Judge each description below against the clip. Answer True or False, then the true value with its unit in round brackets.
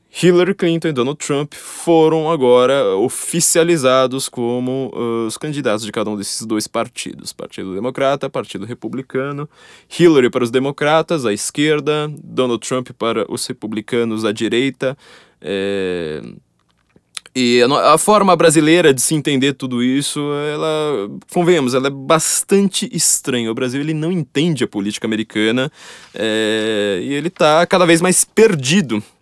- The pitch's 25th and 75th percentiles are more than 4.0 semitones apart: True (5.1 semitones)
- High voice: False (140 Hz)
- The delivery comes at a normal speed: True (140 wpm)